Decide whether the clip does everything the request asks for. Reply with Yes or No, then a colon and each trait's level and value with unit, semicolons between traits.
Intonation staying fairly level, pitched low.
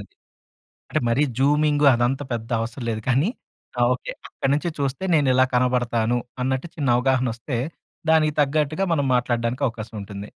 No: average, 3.4 semitones; low, 130 Hz